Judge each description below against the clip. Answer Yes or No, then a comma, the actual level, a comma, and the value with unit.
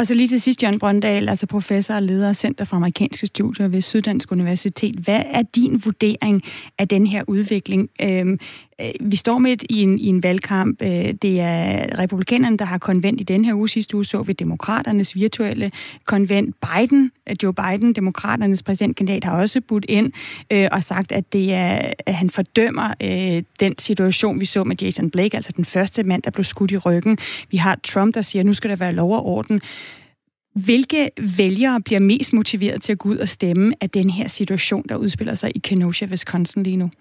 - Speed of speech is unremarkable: Yes, average, 195 wpm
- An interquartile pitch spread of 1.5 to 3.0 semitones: Yes, narrow, 2.4 semitones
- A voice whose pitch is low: No, high, 200 Hz